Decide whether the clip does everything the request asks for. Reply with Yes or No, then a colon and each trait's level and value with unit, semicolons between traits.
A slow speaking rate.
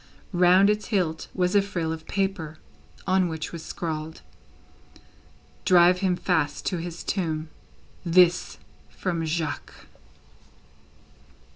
Yes: slow, 110 wpm